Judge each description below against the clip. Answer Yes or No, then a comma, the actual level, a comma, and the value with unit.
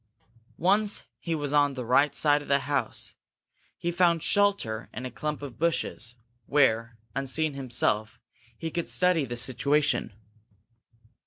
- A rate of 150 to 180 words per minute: No, average, 140 wpm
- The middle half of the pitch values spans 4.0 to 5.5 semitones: Yes, average, 4.4 semitones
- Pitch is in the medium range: Yes, medium, 145 Hz